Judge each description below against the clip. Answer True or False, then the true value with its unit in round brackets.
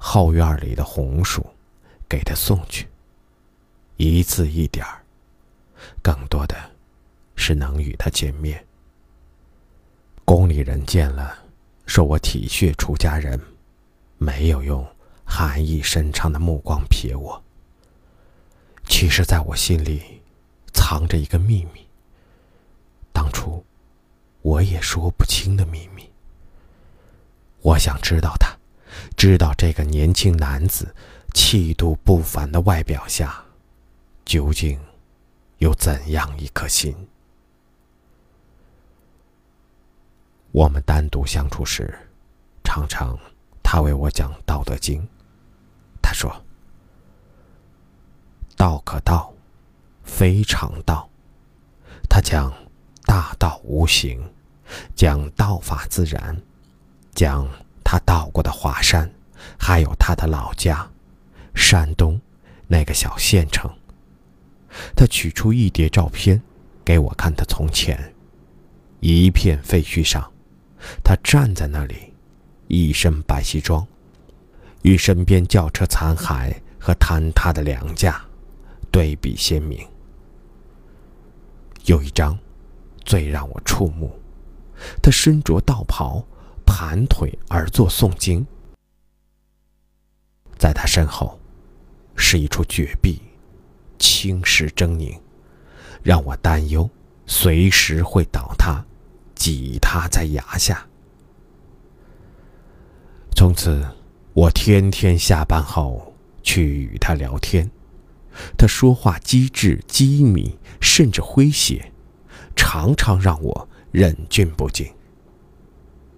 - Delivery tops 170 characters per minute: False (145 characters per minute)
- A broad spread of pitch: False (4.6 semitones)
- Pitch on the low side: True (80 Hz)